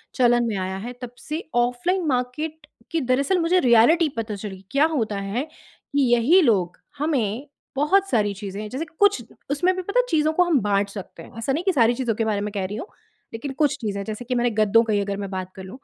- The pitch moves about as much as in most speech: No, wide, 6.8 semitones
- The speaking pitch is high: Yes, high, 240 Hz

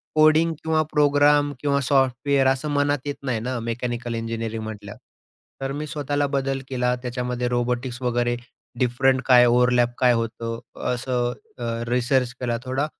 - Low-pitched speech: Yes, low, 125 Hz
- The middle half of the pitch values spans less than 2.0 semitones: No, narrow, 2.6 semitones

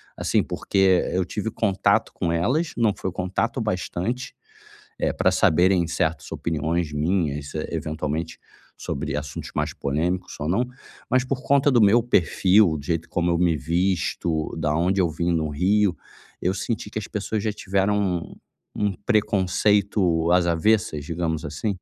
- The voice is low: Yes, very low, 90 Hz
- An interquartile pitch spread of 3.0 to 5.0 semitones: Yes, average, 4.1 semitones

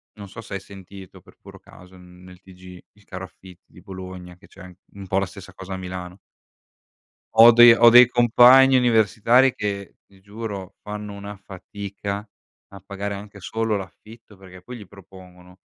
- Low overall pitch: Yes, low, 100 Hz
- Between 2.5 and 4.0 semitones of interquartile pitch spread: Yes, average, 2.8 semitones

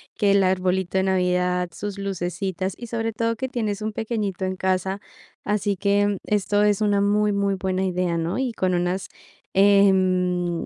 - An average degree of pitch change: No, narrow, 2.1 semitones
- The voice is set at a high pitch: Yes, high, 195 Hz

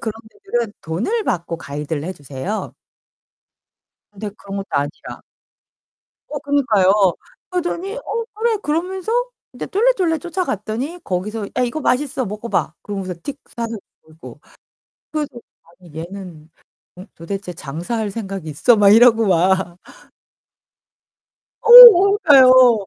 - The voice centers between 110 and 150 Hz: No, high, 220 Hz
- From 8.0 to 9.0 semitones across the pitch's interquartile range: Yes, wide, 8.7 semitones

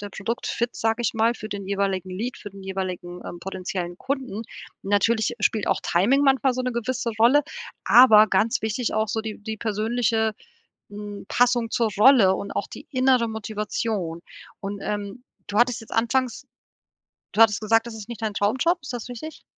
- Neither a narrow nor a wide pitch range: Yes, average, 3.0 semitones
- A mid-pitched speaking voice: No, high, 220 Hz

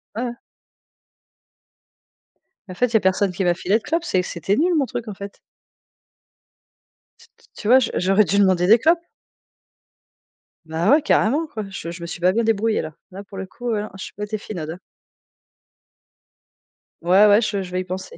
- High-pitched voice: Yes, high, 200 Hz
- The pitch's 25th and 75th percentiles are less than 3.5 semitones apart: No, average, 3.8 semitones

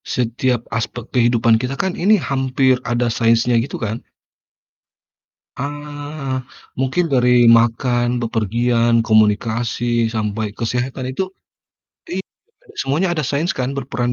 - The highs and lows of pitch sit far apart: No, average, 2.7 semitones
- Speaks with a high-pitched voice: No, low, 125 Hz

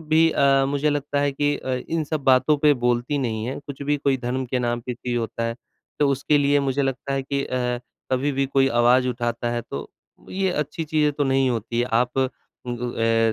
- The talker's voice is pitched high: No, low, 135 Hz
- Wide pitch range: No, average, 2.8 semitones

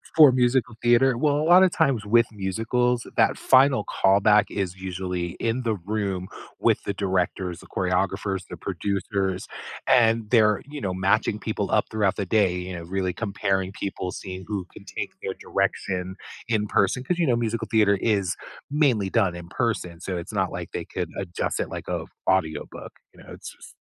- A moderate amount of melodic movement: Yes, average, 3.9 semitones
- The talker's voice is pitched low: Yes, low, 100 Hz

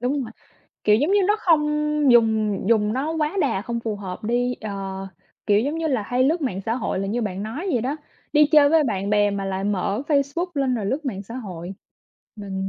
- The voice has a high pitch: Yes, high, 230 Hz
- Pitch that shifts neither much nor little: No, wide, 5.7 semitones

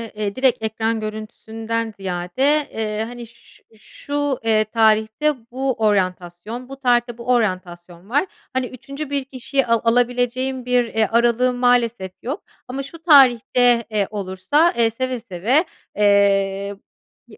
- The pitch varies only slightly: No, average, 3.3 semitones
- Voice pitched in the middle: No, high, 235 Hz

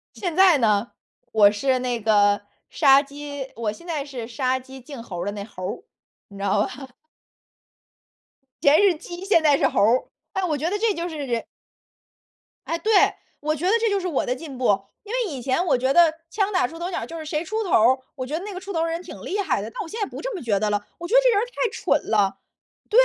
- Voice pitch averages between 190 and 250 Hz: No, very high, 290 Hz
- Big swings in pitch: Yes, wide, 7.2 semitones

